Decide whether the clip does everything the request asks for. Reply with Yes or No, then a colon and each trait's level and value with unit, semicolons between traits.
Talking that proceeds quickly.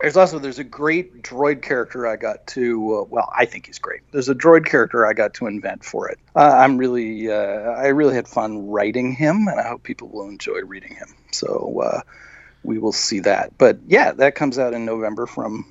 Yes: fast, 220 wpm